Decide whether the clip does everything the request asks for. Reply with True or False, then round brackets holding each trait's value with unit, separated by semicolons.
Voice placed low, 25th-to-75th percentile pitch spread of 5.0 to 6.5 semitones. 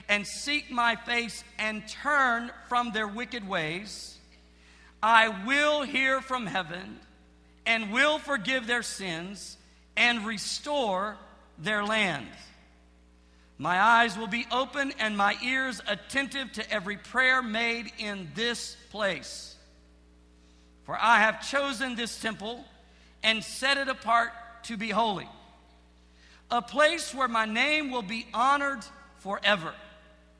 False (220 Hz; 5.6 semitones)